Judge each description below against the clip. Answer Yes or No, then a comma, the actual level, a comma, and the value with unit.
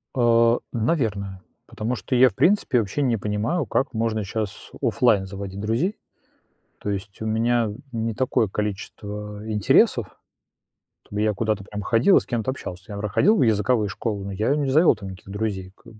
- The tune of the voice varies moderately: Yes, average, 3.0 semitones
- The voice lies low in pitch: Yes, low, 110 Hz